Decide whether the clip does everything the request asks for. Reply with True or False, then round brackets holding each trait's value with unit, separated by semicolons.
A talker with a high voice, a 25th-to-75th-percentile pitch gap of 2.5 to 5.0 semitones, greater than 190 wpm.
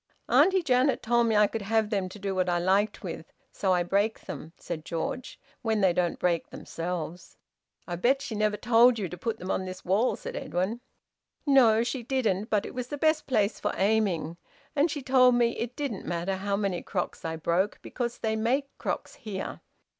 True (210 Hz; 4.7 semitones; 200 wpm)